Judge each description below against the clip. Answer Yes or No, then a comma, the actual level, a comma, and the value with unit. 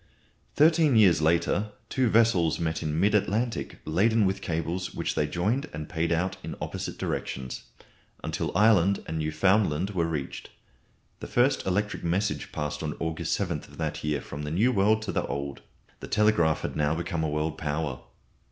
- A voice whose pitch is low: Yes, very low, 85 Hz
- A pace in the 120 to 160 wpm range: No, average, 170 wpm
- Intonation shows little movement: No, wide, 5.4 semitones